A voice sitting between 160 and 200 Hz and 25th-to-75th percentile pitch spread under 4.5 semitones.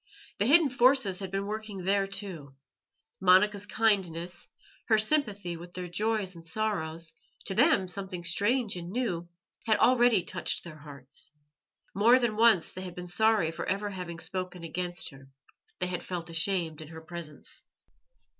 Yes: medium, 185 Hz; average, 3.9 semitones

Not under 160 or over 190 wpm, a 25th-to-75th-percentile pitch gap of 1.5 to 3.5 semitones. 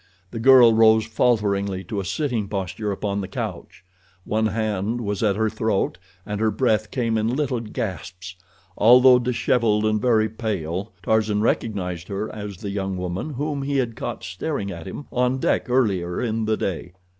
Yes: average, 170 wpm; average, 3.0 semitones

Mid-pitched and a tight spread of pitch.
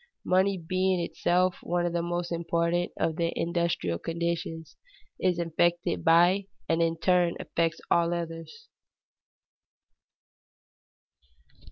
Yes: medium, 170 Hz; narrow, 0.9 semitones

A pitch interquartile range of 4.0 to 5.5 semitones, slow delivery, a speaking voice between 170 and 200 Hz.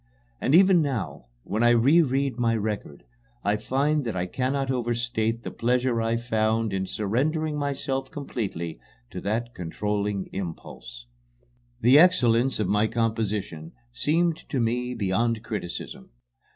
No: average, 4.3 semitones; slow, 130 wpm; low, 115 Hz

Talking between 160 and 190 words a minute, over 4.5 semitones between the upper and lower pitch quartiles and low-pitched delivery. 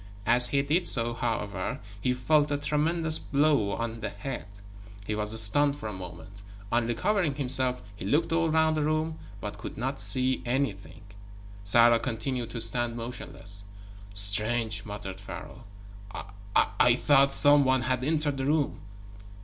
No: average, 150 wpm; average, 4.9 semitones; low, 125 Hz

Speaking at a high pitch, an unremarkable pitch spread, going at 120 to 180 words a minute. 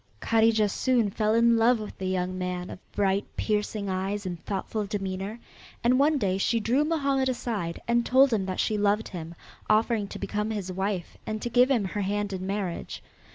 No: high, 210 Hz; average, 3.4 semitones; average, 195 wpm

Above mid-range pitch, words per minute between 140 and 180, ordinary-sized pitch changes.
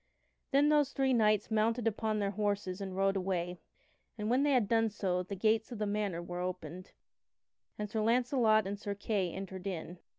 No: high, 210 Hz; average, 190 wpm; average, 3.0 semitones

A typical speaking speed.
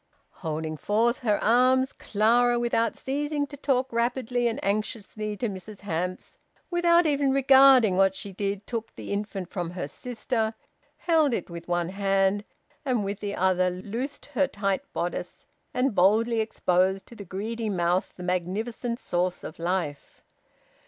Yes: average, 150 wpm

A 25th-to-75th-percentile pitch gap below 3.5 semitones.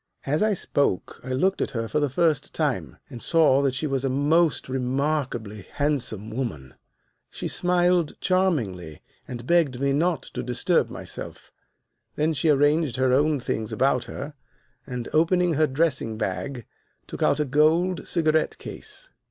No: average, 4.2 semitones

